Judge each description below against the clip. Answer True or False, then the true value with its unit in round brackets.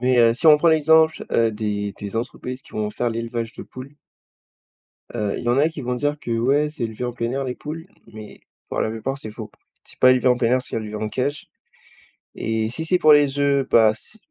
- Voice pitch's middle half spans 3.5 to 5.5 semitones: True (4.2 semitones)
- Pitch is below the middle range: True (125 Hz)